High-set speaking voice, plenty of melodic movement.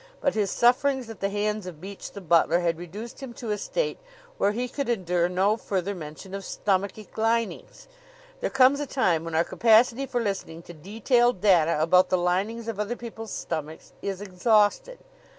No: high, 205 Hz; average, 4.6 semitones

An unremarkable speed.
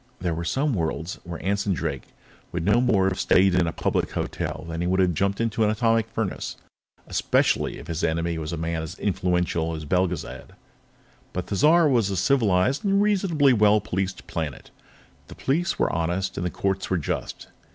Yes: average, 185 wpm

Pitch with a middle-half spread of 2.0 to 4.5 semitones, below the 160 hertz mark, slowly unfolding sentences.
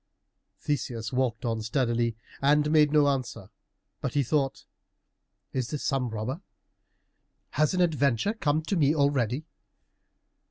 Yes: average, 4.1 semitones; medium, 140 Hz; slow, 125 wpm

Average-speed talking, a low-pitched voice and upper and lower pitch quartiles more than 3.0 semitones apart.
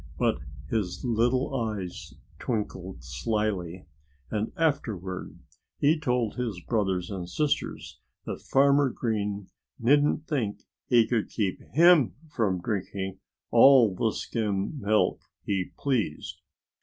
No: slow, 110 wpm; low, 110 Hz; average, 5.1 semitones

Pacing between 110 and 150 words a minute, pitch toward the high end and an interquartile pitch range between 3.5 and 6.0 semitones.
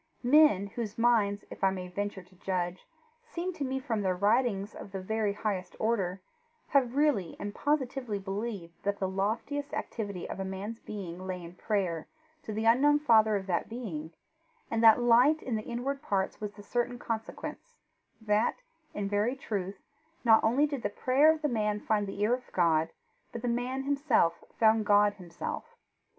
No: average, 180 wpm; high, 215 Hz; average, 4.1 semitones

